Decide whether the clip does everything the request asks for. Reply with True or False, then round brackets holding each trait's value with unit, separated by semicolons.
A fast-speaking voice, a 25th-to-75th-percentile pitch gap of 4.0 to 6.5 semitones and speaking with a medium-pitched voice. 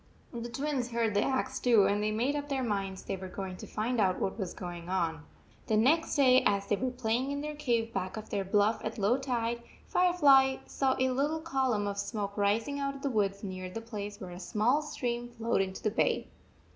False (220 wpm; 4.7 semitones; 230 Hz)